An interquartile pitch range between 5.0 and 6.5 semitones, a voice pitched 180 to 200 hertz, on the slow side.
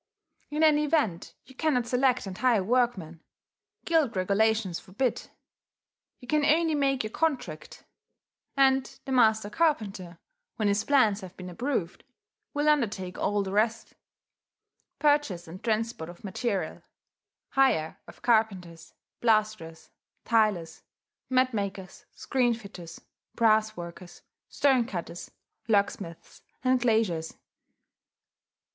No: wide, 5.6 semitones; high, 220 Hz; slow, 115 wpm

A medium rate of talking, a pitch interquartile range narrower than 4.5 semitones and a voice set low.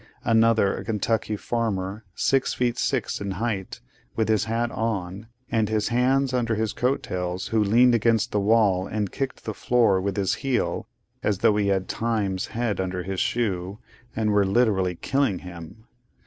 Yes: average, 170 wpm; average, 3.2 semitones; low, 110 Hz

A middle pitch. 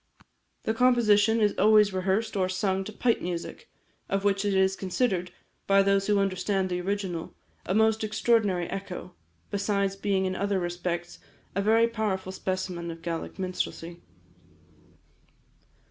No: high, 195 Hz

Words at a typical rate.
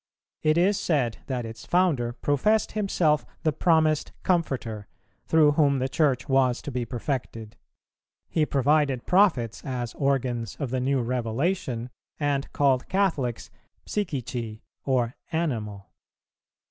No: slow, 120 wpm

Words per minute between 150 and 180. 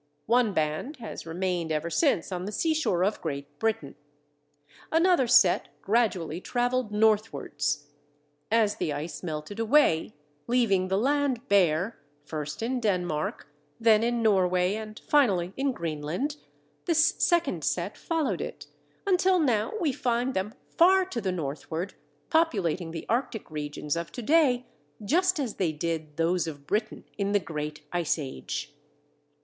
No: average, 140 wpm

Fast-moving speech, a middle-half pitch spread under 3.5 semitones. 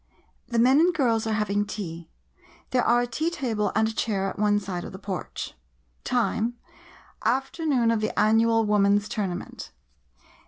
No: average, 165 wpm; average, 2.8 semitones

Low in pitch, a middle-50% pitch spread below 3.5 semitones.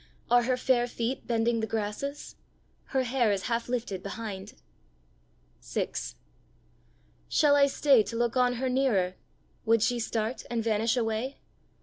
No: high, 235 Hz; narrow, 2.5 semitones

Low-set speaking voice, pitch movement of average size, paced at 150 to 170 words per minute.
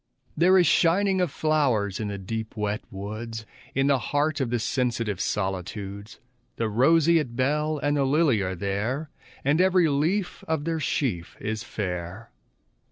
No: low, 125 Hz; wide, 6.8 semitones; average, 155 wpm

